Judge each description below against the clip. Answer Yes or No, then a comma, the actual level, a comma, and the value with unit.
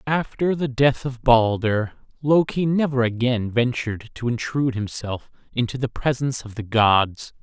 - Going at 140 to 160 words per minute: Yes, average, 145 wpm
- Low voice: Yes, low, 125 Hz